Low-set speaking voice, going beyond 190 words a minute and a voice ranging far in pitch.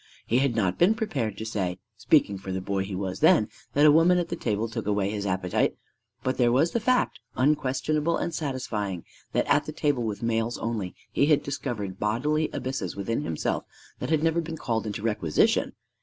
Yes: low, 115 Hz; average, 200 wpm; wide, 6.7 semitones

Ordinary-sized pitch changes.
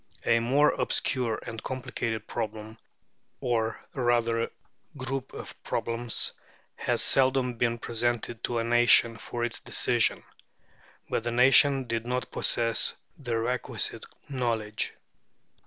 No: narrow, 1.7 semitones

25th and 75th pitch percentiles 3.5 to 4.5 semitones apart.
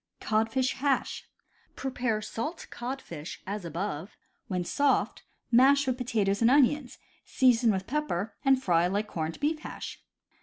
No: wide, 5.4 semitones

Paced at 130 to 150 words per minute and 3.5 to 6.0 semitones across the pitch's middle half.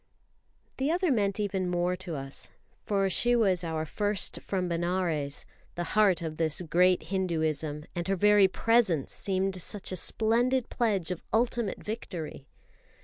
Yes: average, 145 wpm; average, 3.8 semitones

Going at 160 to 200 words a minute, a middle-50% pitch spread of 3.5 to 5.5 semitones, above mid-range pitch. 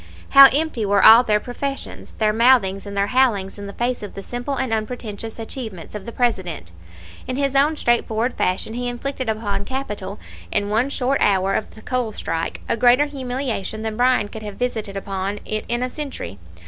Yes: average, 190 wpm; average, 3.8 semitones; high, 225 Hz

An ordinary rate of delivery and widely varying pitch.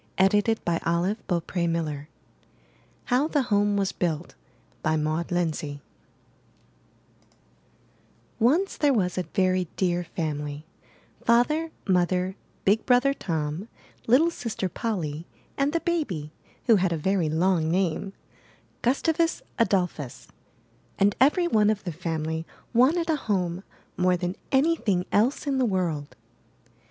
No: slow, 120 wpm; wide, 6.4 semitones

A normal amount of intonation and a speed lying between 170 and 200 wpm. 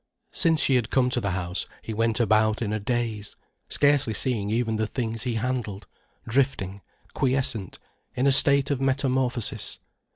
No: average, 3.5 semitones; average, 160 wpm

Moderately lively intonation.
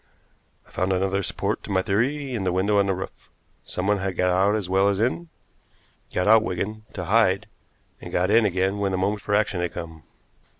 No: narrow, 2.3 semitones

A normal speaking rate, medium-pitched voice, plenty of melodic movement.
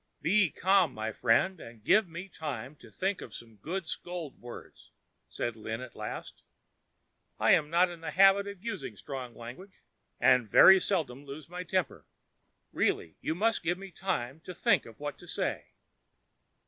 Yes: average, 170 wpm; medium, 160 Hz; wide, 7.4 semitones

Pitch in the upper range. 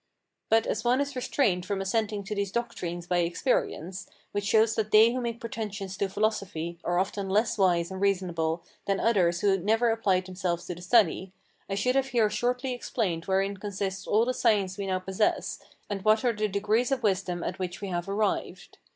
Yes: high, 200 Hz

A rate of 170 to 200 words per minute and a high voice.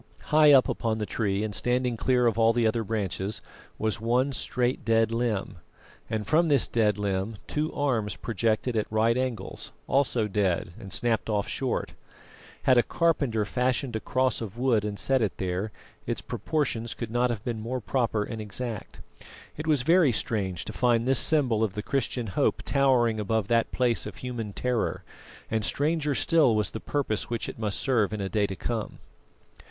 No: average, 185 wpm; low, 115 Hz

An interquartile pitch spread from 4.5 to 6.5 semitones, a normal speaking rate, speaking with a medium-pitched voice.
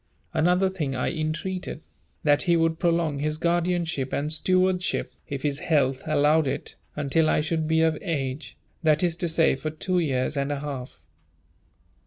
No: average, 2.9 semitones; average, 165 wpm; medium, 155 Hz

